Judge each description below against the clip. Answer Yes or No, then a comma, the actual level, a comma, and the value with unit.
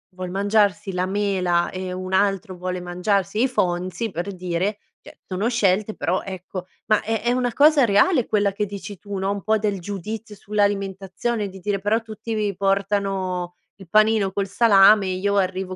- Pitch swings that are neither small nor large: No, narrow, 2.3 semitones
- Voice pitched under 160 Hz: No, high, 200 Hz